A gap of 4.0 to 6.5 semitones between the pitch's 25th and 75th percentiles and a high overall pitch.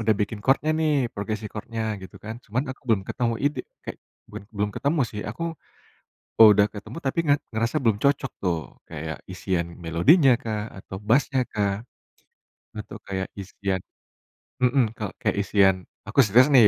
No: average, 4.8 semitones; low, 110 Hz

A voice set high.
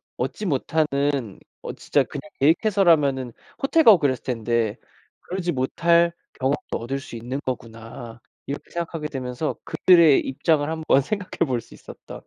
No: medium, 140 Hz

